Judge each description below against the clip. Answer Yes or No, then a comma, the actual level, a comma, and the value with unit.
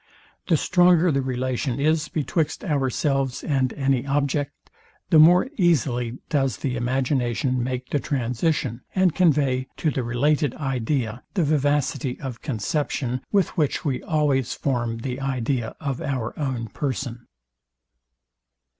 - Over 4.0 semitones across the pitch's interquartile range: No, average, 3.2 semitones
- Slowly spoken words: Yes, slow, 130 wpm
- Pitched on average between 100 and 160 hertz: Yes, low, 135 Hz